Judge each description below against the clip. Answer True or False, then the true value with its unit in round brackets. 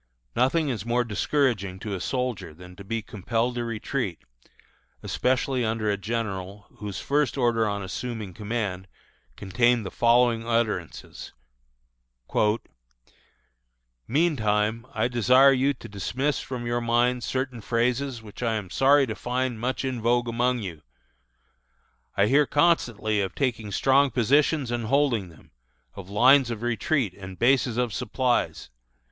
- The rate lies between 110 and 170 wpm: True (140 wpm)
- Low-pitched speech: True (120 Hz)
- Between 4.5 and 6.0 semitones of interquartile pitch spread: False (3.4 semitones)